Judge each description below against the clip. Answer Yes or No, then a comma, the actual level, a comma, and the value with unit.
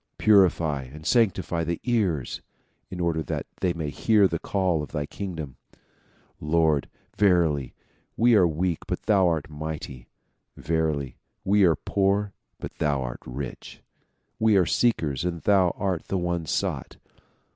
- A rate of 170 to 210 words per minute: No, average, 145 wpm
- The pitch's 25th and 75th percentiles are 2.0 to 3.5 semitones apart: No, average, 4.3 semitones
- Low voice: Yes, very low, 85 Hz